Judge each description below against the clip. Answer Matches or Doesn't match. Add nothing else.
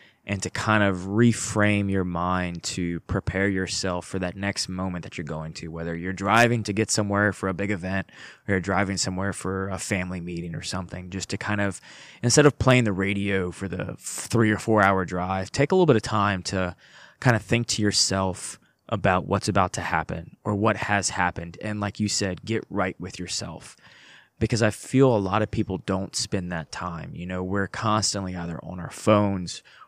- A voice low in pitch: Matches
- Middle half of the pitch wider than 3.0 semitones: Doesn't match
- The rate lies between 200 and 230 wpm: Matches